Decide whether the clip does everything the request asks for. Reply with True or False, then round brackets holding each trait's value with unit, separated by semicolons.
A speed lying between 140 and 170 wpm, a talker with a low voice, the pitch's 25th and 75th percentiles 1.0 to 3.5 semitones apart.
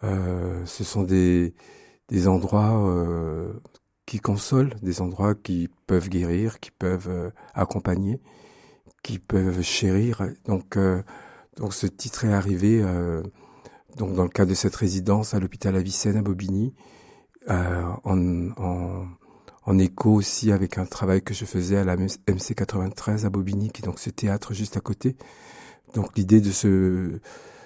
True (150 wpm; 95 Hz; 2.6 semitones)